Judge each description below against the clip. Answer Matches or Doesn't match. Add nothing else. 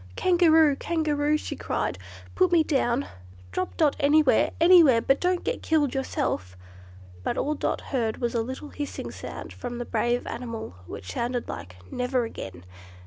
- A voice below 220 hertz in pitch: Doesn't match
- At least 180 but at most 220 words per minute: Doesn't match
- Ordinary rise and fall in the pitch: Matches